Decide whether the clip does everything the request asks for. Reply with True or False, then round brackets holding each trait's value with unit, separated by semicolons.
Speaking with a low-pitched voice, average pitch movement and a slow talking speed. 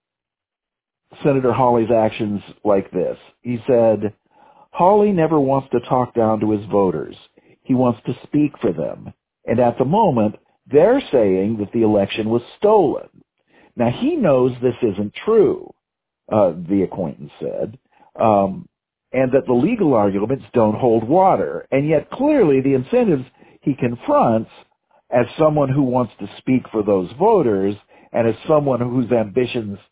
False (125 Hz; 4.9 semitones; 145 wpm)